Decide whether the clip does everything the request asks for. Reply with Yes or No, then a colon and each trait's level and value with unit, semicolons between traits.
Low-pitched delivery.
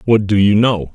Yes: low, 105 Hz